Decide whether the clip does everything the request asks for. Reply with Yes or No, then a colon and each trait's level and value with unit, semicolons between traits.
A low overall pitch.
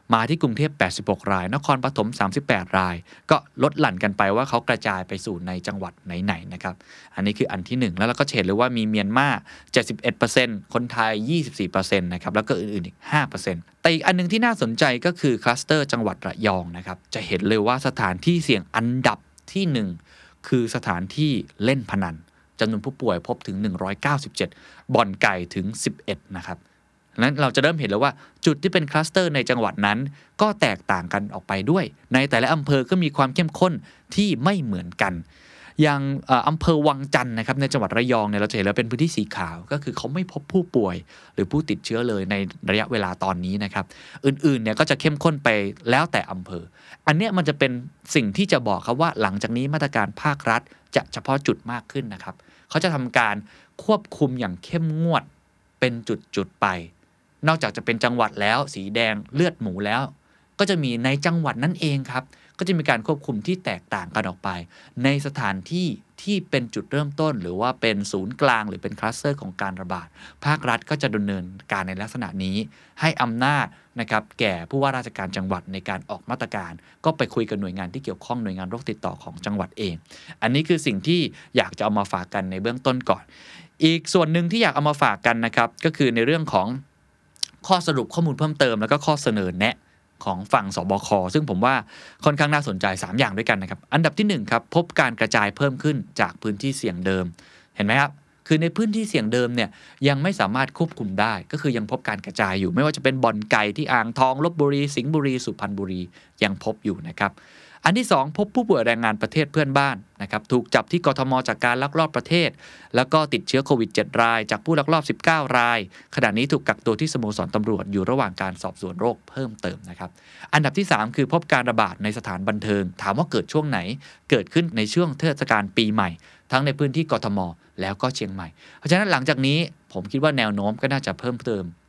Yes: low, 120 Hz